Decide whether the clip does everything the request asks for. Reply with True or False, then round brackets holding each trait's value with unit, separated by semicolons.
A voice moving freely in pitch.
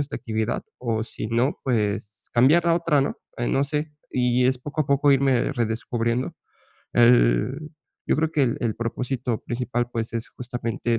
False (2.9 semitones)